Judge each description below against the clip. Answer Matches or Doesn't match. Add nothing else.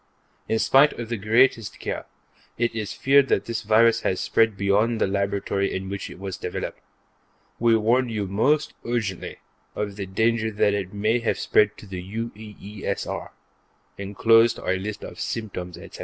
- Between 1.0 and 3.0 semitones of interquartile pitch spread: Matches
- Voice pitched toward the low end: Matches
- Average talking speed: Matches